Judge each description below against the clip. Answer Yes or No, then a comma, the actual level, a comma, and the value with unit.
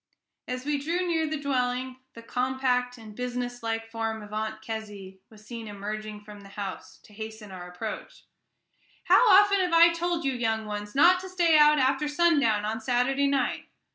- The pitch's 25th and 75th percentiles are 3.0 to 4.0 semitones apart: No, average, 5.3 semitones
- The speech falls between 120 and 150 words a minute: No, average, 175 wpm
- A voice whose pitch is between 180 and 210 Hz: No, high, 245 Hz